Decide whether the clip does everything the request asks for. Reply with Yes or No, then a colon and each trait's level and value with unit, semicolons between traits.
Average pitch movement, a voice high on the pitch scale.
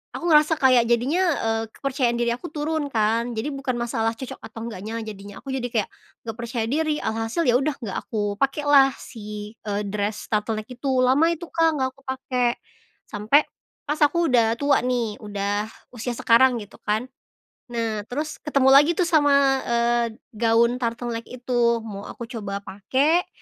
Yes: average, 3.7 semitones; high, 240 Hz